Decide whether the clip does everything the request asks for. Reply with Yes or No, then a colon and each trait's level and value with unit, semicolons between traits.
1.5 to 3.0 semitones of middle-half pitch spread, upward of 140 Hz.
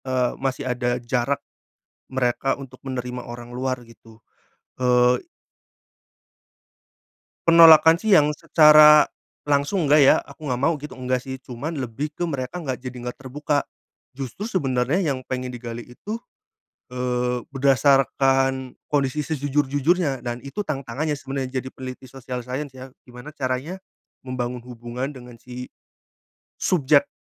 No: narrow, 2.6 semitones; low, 130 Hz